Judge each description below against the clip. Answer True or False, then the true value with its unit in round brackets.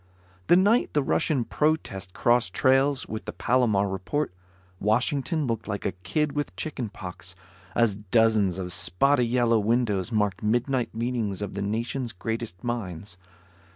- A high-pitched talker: False (115 Hz)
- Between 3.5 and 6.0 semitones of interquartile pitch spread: True (4.5 semitones)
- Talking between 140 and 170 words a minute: True (145 wpm)